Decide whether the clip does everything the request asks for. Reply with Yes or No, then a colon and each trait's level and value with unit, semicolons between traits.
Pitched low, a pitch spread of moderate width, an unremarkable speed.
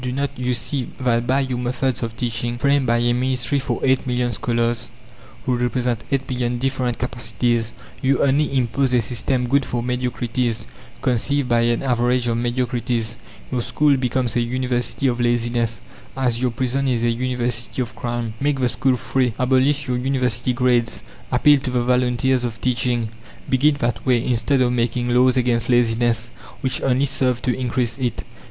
No: low, 125 Hz; narrow, 1.5 semitones; average, 175 wpm